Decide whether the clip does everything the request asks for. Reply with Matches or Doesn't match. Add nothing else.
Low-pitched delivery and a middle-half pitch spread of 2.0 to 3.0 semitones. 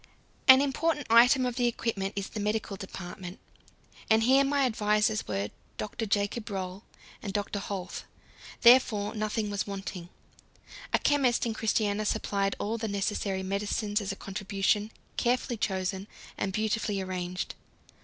Doesn't match